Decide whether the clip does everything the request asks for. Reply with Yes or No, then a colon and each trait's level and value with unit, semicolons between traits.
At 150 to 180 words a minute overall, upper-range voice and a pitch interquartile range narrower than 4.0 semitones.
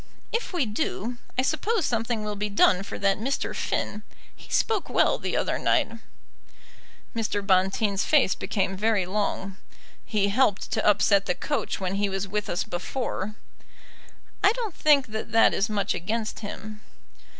Yes: average, 160 wpm; high, 210 Hz; average, 3.4 semitones